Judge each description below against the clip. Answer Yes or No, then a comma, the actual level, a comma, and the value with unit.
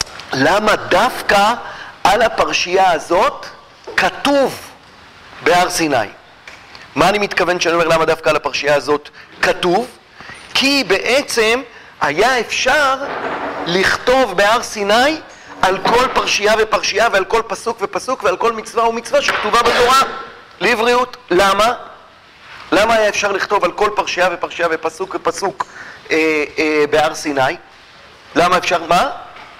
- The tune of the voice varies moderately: No, wide, 6.2 semitones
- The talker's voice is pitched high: Yes, high, 205 Hz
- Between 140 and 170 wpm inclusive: No, average, 120 wpm